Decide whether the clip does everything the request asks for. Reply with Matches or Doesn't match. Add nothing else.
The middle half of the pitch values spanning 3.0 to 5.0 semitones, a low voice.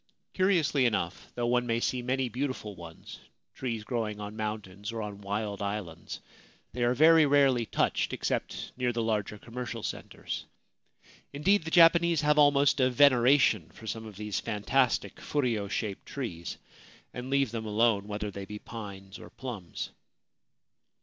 Matches